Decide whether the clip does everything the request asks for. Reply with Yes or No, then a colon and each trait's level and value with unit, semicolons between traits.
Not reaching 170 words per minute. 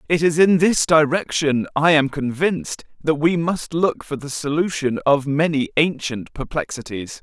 Yes: average, 160 wpm